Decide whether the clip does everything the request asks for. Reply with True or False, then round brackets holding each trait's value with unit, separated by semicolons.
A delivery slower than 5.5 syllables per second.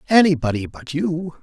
True (5.0 syllables/s)